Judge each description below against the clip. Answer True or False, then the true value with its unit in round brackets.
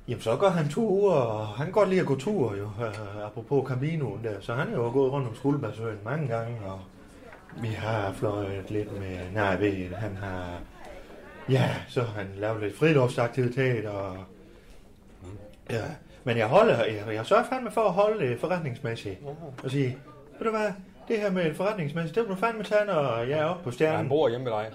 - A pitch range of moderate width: False (6.7 semitones)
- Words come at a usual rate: True (205 wpm)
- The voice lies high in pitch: False (125 Hz)